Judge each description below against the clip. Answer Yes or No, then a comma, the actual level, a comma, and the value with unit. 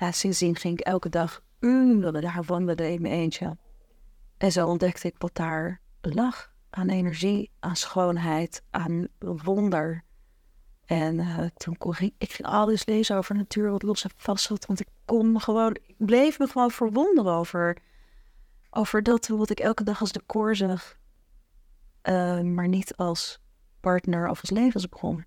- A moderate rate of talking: Yes, average, 170 wpm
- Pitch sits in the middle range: Yes, medium, 180 Hz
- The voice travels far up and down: No, average, 3.9 semitones